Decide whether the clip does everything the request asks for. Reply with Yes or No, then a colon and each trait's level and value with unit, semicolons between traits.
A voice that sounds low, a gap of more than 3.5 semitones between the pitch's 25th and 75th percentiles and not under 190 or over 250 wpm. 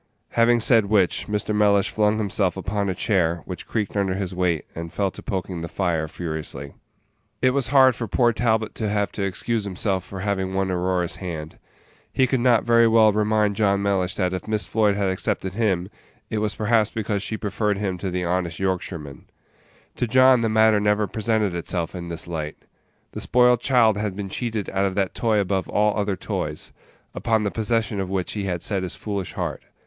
No: low, 100 Hz; average, 2.9 semitones; average, 200 wpm